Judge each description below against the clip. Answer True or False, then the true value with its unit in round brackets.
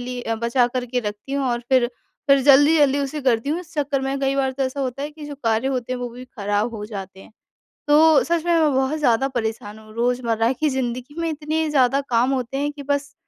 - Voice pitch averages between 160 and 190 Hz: False (265 Hz)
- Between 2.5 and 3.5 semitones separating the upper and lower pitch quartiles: True (3.2 semitones)